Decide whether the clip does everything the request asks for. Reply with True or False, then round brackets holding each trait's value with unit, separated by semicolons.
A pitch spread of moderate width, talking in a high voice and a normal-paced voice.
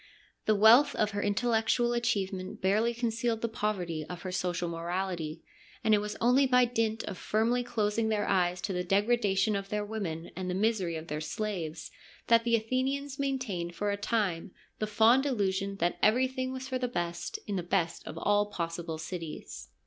True (4.5 semitones; 205 Hz; 190 wpm)